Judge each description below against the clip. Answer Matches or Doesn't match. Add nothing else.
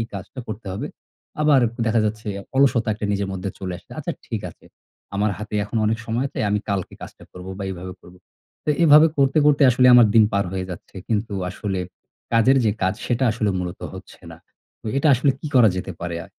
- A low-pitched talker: Matches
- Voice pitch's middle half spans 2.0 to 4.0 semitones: Doesn't match